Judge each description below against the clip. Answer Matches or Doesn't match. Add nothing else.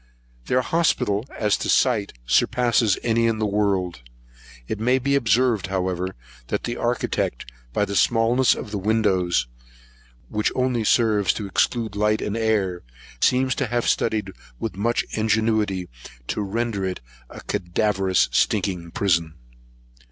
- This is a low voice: Matches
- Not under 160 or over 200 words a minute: Doesn't match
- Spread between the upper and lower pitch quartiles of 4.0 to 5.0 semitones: Doesn't match